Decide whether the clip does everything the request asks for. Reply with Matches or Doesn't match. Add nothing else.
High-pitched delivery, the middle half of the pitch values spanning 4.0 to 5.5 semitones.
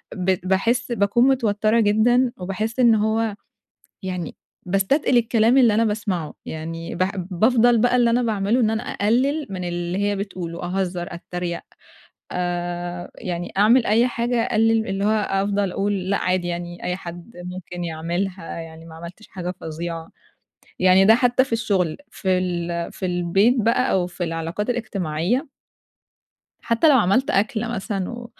Matches